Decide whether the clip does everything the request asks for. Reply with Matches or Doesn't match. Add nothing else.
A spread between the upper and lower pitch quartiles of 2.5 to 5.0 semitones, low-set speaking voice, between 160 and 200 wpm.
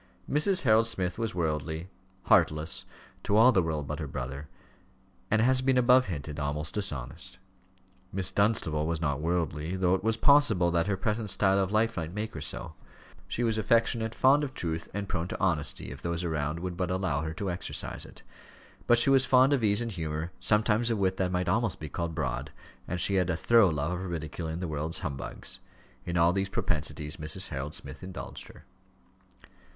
Doesn't match